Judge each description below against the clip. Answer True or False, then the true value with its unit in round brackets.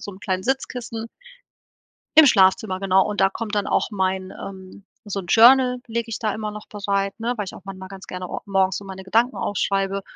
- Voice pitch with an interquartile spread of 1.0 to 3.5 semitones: True (2.7 semitones)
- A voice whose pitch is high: True (200 Hz)